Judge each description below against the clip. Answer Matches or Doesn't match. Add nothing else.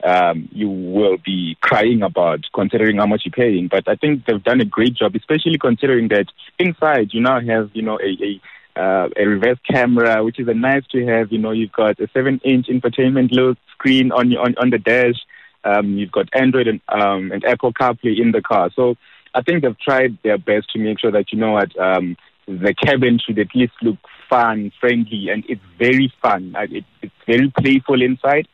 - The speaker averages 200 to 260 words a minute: Matches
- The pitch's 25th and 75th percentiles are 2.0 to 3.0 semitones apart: Doesn't match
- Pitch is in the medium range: Doesn't match